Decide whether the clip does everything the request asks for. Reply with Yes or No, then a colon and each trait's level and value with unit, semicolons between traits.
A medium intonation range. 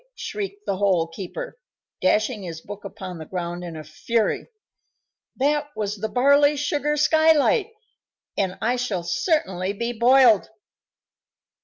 No: wide, 7.8 semitones